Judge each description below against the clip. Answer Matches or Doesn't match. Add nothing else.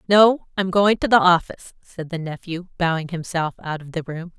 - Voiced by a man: Doesn't match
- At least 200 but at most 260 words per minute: Matches